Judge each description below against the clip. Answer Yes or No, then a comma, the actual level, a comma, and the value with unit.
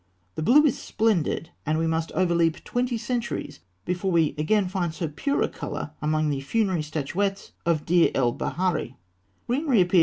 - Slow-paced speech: No, average, 155 wpm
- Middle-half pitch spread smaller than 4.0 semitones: No, average, 4.6 semitones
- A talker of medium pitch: Yes, medium, 170 Hz